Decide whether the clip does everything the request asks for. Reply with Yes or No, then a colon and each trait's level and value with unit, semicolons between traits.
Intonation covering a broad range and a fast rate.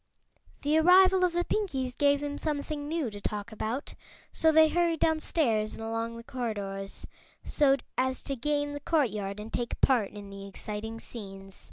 No: wide, 6.2 semitones; average, 170 wpm